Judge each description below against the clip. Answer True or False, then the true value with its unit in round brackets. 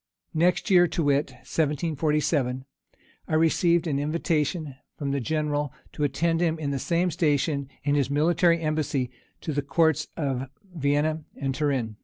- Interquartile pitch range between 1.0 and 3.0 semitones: True (2.7 semitones)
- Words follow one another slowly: False (150 wpm)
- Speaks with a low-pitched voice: False (150 Hz)